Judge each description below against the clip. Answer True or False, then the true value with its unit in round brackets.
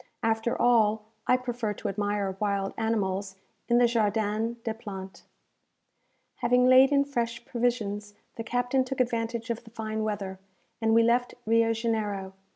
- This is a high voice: True (225 Hz)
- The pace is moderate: True (150 wpm)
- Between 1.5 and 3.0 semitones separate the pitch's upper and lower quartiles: True (2.4 semitones)